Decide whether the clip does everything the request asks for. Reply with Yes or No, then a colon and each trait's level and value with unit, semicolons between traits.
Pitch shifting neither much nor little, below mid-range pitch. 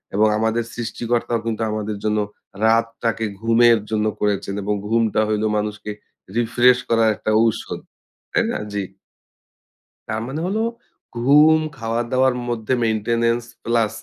No: narrow, 1.6 semitones; low, 115 Hz